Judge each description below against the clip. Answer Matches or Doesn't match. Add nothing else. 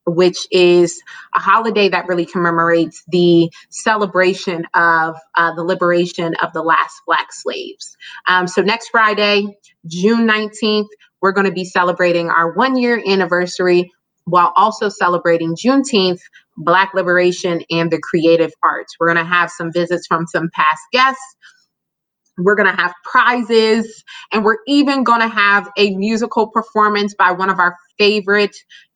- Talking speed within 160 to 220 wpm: Doesn't match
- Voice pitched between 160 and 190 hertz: Matches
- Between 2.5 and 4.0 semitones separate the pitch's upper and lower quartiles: Matches